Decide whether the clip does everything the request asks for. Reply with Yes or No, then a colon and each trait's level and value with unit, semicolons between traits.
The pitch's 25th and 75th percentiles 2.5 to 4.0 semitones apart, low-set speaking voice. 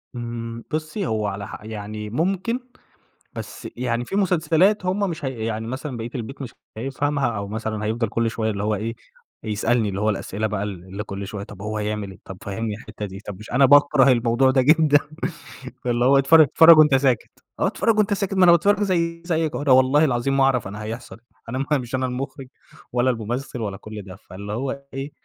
No: average, 5.2 semitones; low, 120 Hz